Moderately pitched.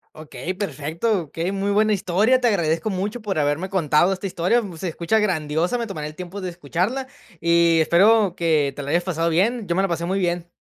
Yes: medium, 180 Hz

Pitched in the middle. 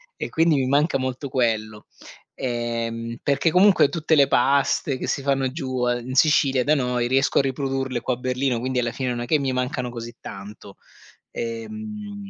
No: low, 130 Hz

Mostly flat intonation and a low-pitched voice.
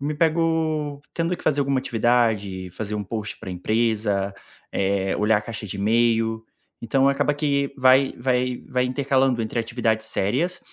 No: average, 4.3 semitones; low, 120 Hz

